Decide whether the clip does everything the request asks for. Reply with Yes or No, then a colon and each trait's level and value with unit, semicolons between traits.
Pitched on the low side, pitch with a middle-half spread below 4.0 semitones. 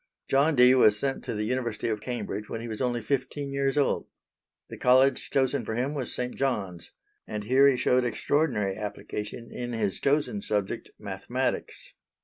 No: low, 125 Hz; average, 4.3 semitones